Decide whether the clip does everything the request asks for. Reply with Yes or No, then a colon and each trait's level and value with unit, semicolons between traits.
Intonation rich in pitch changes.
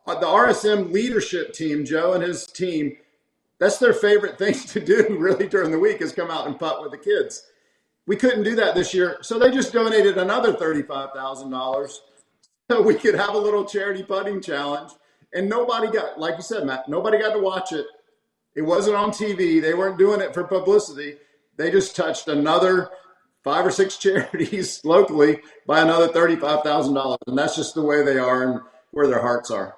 Yes: wide, 6.1 semitones